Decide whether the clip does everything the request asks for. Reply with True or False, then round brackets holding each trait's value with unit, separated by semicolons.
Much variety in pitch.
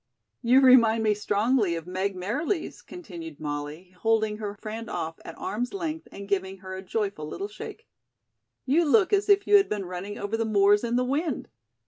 True (5.7 semitones)